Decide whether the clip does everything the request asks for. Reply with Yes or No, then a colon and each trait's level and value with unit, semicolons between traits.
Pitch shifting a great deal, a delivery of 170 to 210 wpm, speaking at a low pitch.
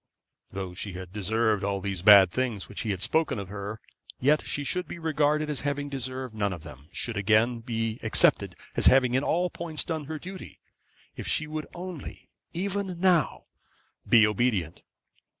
Yes: wide, 7.1 semitones; average, 175 wpm; low, 120 Hz